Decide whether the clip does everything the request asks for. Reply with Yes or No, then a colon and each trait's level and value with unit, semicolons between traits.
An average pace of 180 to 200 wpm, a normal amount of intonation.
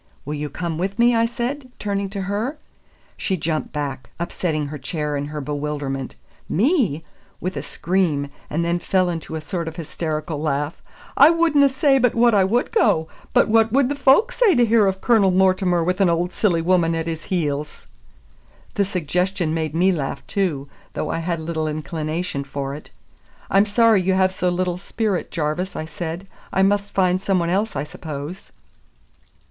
Yes: average, 185 wpm; average, 4.5 semitones